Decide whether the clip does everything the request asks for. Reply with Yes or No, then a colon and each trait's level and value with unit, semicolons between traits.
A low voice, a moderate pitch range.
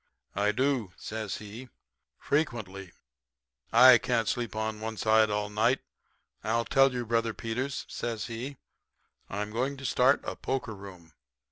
Yes: low, 115 Hz; average, 3.0 semitones